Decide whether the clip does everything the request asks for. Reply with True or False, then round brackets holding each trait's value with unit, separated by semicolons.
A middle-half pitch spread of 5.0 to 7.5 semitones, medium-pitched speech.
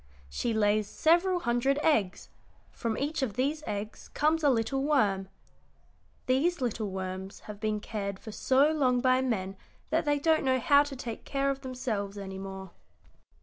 False (5.5 semitones; 250 Hz)